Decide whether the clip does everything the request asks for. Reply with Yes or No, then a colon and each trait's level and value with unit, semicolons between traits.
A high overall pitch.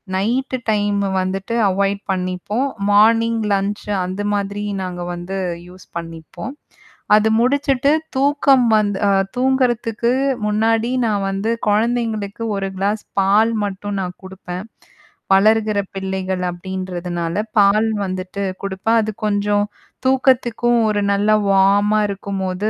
Yes: high, 205 Hz